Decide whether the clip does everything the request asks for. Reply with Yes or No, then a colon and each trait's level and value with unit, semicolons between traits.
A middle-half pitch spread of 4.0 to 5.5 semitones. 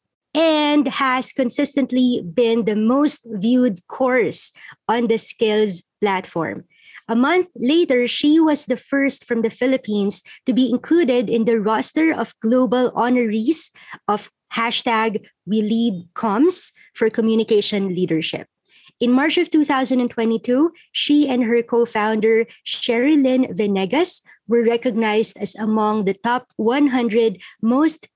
No: average, 3.4 semitones